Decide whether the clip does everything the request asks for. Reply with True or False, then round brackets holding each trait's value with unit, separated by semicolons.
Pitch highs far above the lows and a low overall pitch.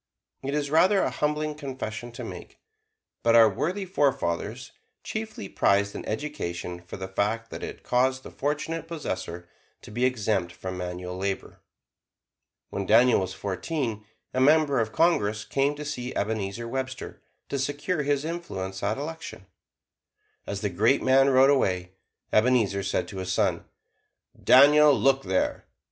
True (6.6 semitones; 125 Hz)